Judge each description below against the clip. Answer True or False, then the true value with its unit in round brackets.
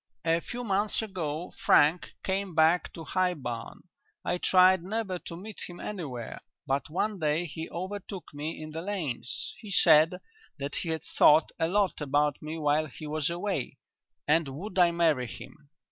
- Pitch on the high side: False (165 Hz)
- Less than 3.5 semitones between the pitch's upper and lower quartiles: False (3.8 semitones)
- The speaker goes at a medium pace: True (170 wpm)